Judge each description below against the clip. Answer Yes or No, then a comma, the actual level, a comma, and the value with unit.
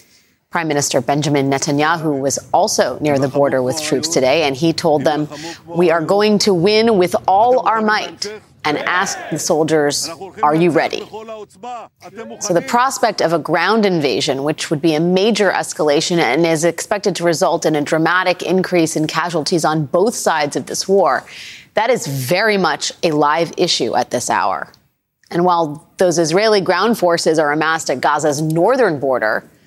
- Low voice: No, medium, 170 Hz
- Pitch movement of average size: Yes, average, 4.0 semitones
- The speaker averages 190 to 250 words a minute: No, average, 170 wpm